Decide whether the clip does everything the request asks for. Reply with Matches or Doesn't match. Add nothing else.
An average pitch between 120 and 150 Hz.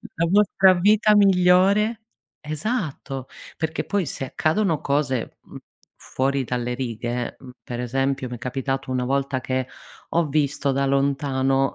Matches